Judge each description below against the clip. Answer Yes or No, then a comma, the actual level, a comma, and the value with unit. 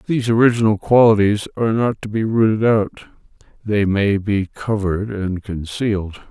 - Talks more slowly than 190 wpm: Yes, average, 145 wpm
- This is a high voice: No, low, 105 Hz